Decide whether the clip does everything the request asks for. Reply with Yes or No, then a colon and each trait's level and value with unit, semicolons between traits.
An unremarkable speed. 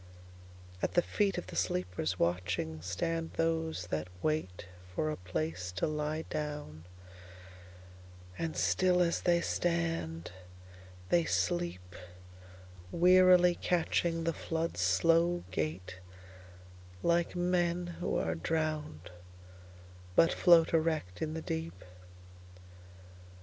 No: slow, 90 wpm